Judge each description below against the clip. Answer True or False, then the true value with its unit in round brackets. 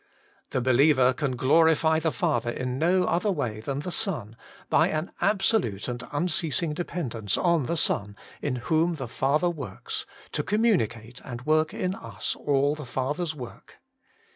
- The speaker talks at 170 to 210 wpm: False (155 wpm)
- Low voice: False (145 Hz)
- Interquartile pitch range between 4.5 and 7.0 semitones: True (5.3 semitones)